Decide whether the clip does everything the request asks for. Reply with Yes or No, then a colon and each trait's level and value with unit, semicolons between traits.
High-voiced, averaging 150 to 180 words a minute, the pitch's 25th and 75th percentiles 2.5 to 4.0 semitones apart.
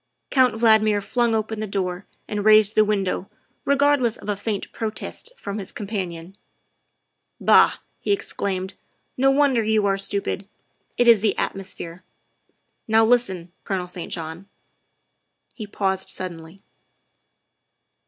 Yes: high, 205 Hz; average, 155 wpm; average, 2.8 semitones